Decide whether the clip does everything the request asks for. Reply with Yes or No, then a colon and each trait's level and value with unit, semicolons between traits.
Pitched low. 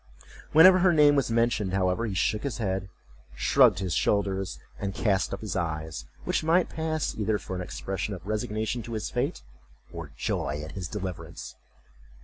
Yes: low, 105 Hz